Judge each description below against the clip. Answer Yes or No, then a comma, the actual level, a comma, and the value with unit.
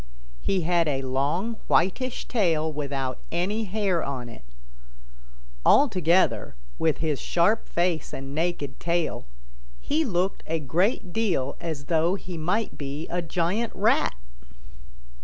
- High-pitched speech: No, medium, 170 Hz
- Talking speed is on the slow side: Yes, slow, 125 wpm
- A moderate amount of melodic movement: Yes, average, 4.5 semitones